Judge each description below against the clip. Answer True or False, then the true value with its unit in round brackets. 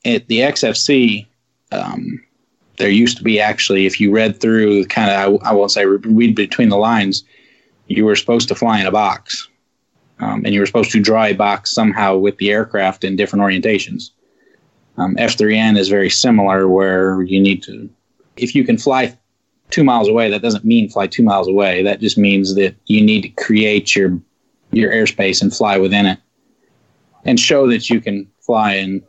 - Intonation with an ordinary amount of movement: False (2.2 semitones)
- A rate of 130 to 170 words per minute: False (190 wpm)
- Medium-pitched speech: False (100 Hz)